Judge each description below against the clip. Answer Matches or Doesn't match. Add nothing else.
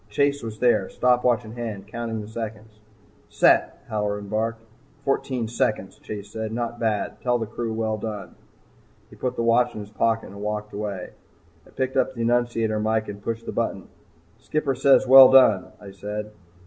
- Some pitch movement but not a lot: Doesn't match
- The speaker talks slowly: Doesn't match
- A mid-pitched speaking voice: Doesn't match